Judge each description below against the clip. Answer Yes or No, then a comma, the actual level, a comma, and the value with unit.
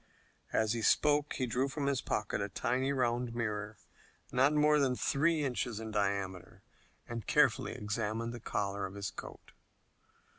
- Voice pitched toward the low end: Yes, low, 120 Hz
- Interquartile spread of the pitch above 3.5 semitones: Yes, average, 4.4 semitones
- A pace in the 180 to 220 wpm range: No, average, 155 wpm